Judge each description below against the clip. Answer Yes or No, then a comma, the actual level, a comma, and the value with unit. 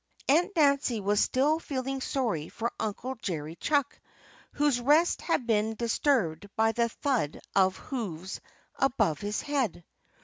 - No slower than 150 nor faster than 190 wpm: No, slow, 135 wpm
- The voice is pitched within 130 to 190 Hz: No, high, 235 Hz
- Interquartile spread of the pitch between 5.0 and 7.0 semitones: Yes, wide, 5.5 semitones